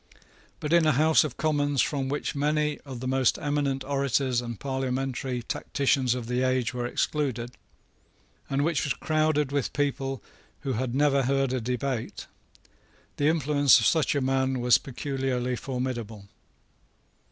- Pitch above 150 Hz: No, low, 135 Hz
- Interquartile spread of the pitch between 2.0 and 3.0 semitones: Yes, narrow, 2.4 semitones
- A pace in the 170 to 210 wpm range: No, average, 150 wpm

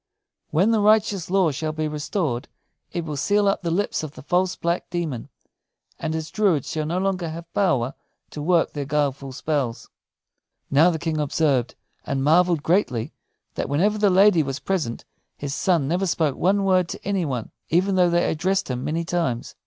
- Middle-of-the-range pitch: Yes, medium, 165 Hz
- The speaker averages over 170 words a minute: Yes, average, 185 wpm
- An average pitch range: Yes, average, 4.3 semitones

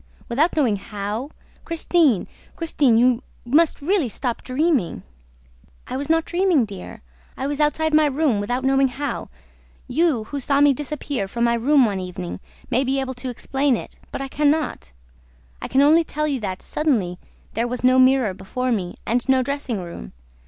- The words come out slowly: No, average, 175 wpm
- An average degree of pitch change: Yes, average, 4.1 semitones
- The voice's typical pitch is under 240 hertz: No, very high, 265 Hz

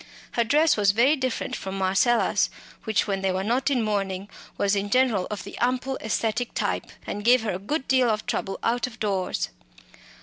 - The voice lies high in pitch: Yes, high, 220 Hz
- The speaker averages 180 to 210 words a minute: Yes, average, 195 wpm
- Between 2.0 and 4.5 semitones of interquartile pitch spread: Yes, average, 4.1 semitones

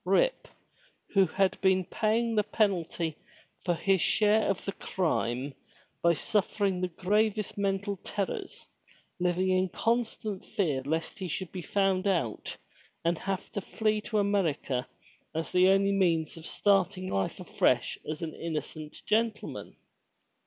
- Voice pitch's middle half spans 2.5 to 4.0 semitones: Yes, average, 3.3 semitones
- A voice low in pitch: No, high, 190 Hz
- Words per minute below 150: Yes, average, 140 wpm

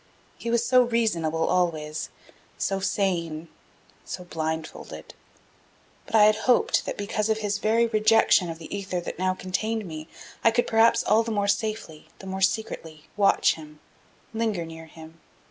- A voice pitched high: Yes, high, 195 Hz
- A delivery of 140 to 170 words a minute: Yes, average, 160 wpm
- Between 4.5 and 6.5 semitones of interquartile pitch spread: Yes, average, 5.2 semitones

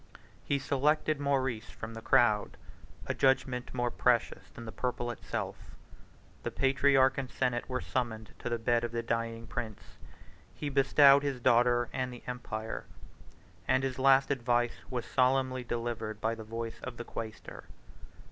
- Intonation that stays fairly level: Yes, narrow, 2.3 semitones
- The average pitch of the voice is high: No, low, 125 Hz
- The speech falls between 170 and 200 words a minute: No, average, 155 wpm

